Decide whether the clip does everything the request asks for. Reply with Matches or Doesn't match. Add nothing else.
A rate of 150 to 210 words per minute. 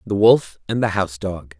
Doesn't match